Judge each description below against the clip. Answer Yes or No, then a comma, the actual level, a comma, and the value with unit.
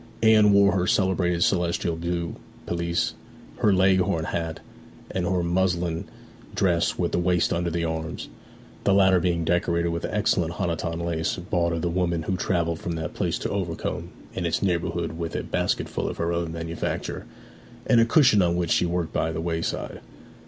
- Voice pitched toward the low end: Yes, very low, 85 Hz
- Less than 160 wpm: No, average, 175 wpm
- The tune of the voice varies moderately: No, narrow, 1.7 semitones